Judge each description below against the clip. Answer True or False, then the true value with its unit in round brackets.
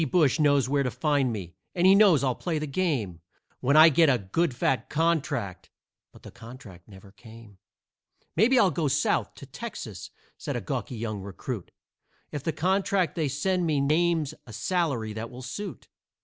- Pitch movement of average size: False (6.4 semitones)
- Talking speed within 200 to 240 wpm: False (180 wpm)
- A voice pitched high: False (140 Hz)